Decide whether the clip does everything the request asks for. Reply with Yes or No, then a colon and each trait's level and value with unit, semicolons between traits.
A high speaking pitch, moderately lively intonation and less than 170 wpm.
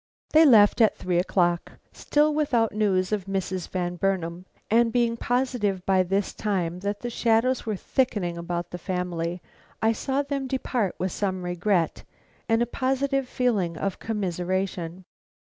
Yes: high, 200 Hz; average, 4.9 semitones; average, 150 wpm